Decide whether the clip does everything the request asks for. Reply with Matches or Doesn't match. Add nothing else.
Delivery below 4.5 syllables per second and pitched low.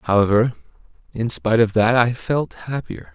Doesn't match